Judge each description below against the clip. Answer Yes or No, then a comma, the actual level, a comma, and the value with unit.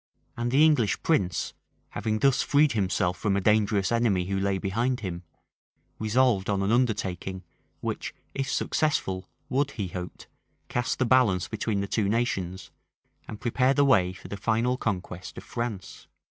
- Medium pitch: No, low, 110 Hz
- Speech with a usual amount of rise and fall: Yes, average, 4.4 semitones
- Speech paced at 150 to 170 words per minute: Yes, average, 160 wpm